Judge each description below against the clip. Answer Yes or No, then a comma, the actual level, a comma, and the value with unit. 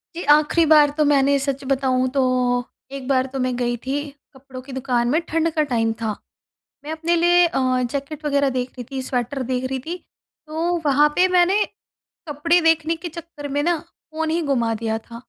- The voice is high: Yes, very high, 285 Hz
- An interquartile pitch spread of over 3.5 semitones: Yes, average, 3.9 semitones